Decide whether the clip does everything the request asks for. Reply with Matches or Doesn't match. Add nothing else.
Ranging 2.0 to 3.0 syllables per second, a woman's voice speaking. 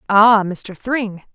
Matches